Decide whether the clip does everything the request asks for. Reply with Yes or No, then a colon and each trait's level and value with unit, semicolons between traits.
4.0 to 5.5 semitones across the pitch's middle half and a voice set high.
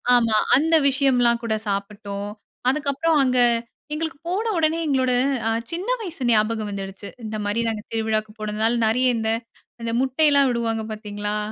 Yes: average, 4.7 semitones; high, 230 Hz